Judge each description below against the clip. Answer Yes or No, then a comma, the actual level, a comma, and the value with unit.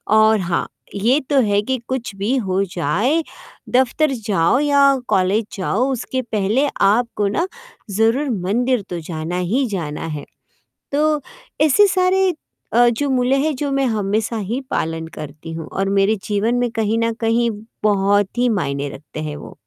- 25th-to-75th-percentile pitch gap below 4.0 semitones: No, average, 5.2 semitones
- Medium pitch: No, high, 220 Hz